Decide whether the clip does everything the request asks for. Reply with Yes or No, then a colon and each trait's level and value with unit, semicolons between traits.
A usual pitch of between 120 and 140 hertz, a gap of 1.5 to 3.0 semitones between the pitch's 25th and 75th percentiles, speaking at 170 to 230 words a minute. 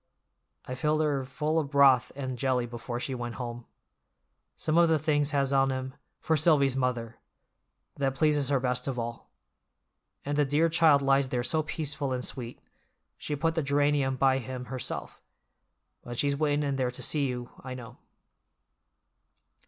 No: low, 135 Hz; average, 2.7 semitones; average, 160 wpm